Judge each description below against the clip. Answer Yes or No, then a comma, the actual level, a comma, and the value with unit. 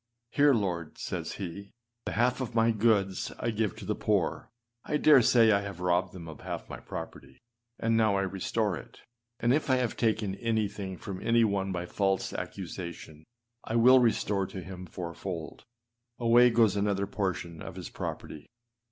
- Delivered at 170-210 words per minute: Yes, average, 185 wpm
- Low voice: Yes, low, 105 Hz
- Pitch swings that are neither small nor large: Yes, average, 3.7 semitones